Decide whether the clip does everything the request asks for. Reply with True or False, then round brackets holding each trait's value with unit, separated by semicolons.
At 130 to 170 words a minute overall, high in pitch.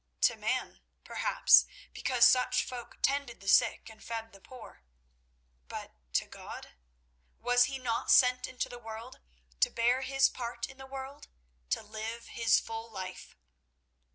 True (145 wpm; 235 Hz)